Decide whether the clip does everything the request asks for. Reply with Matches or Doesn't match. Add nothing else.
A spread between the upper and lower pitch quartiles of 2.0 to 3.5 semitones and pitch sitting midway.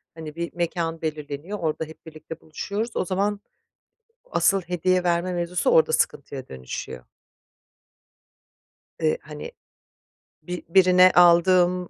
Matches